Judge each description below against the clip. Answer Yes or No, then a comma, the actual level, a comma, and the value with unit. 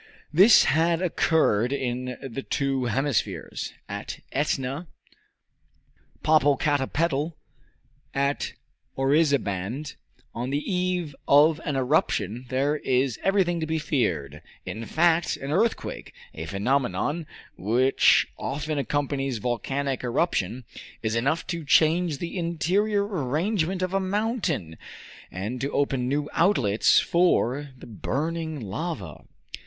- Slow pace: Yes, slow, 110 wpm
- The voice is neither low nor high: Yes, medium, 145 Hz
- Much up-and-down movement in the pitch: No, average, 4.8 semitones